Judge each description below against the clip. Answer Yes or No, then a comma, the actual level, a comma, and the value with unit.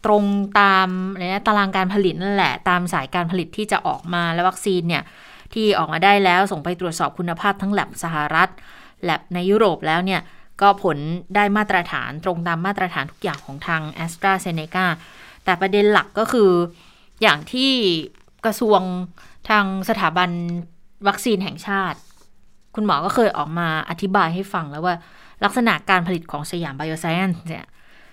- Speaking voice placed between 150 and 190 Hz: Yes, medium, 185 Hz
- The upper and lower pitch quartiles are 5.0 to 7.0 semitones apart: No, average, 2.9 semitones